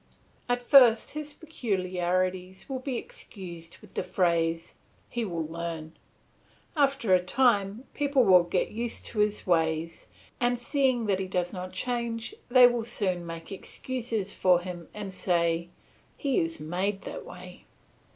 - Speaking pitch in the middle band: No, high, 195 Hz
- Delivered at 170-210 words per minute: No, average, 145 wpm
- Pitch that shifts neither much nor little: No, wide, 5.7 semitones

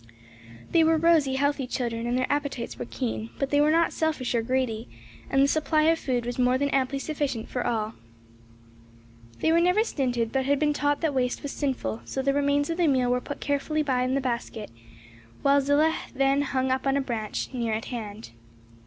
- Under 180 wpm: No, fast, 205 wpm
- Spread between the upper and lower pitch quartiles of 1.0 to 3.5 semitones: Yes, average, 2.9 semitones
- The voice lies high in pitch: Yes, very high, 270 Hz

